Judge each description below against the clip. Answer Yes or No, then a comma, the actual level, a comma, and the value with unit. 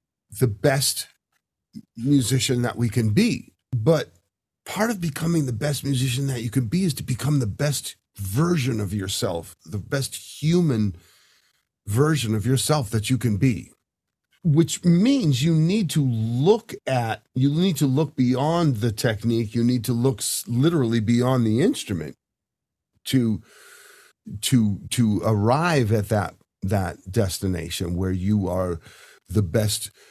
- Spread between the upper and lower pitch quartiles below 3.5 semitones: No, average, 5.3 semitones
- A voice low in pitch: Yes, low, 125 Hz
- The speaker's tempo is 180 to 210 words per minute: No, average, 140 wpm